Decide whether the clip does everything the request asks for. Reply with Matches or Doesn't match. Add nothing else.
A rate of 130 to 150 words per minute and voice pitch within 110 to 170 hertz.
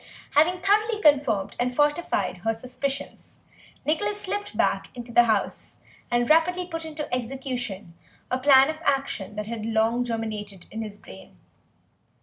Doesn't match